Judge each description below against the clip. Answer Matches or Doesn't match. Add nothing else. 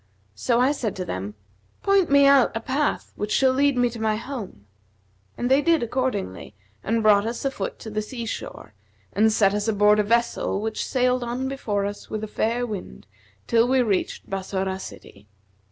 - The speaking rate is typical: Matches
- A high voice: Matches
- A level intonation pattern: Doesn't match